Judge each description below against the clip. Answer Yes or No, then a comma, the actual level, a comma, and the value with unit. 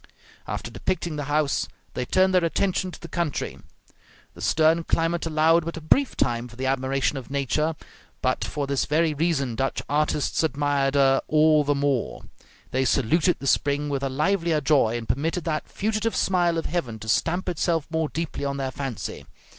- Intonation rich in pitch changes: No, average, 3.5 semitones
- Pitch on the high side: No, medium, 150 Hz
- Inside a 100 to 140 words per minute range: No, average, 180 wpm